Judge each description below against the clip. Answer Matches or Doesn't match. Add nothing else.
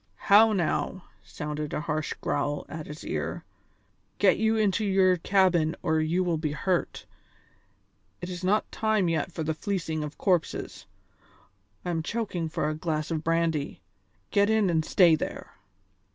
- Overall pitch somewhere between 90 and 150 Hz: Doesn't match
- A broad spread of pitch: Doesn't match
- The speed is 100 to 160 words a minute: Matches